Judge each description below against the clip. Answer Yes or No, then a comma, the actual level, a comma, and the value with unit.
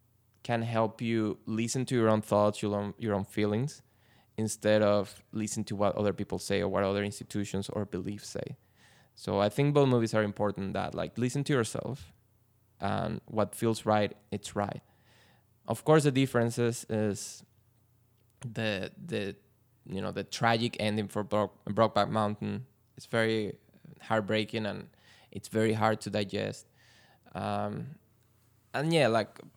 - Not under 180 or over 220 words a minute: No, average, 150 wpm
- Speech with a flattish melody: Yes, narrow, 2.1 semitones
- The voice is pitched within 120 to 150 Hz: No, low, 110 Hz